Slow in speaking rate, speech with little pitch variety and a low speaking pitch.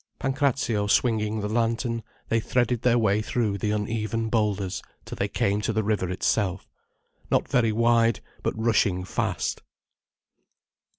Yes: slow, 130 wpm; narrow, 2.0 semitones; low, 110 Hz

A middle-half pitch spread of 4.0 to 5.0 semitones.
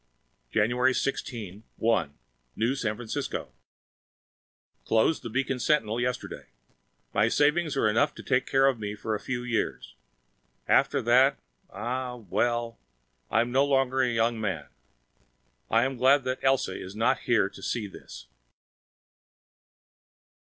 No: average, 3.2 semitones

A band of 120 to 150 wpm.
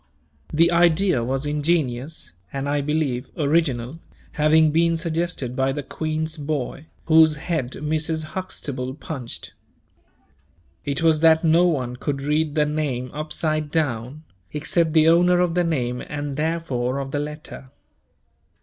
Yes: slow, 135 wpm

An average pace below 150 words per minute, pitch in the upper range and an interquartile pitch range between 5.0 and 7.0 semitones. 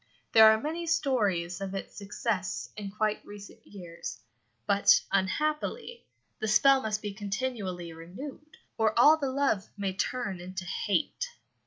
Yes: average, 140 wpm; high, 210 Hz; wide, 5.5 semitones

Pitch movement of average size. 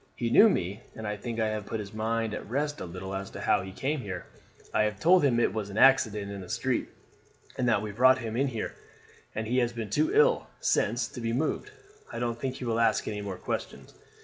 Yes: average, 3.6 semitones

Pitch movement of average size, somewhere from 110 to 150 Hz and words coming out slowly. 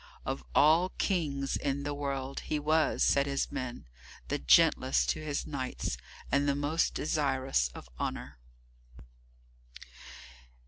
No: narrow, 2.0 semitones; medium, 140 Hz; slow, 125 wpm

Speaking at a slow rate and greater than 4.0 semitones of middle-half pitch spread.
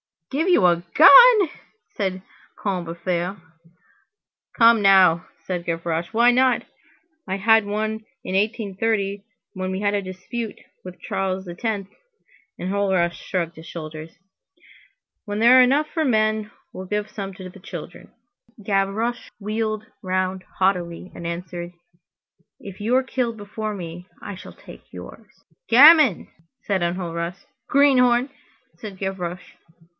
No: slow, 130 wpm; average, 3.6 semitones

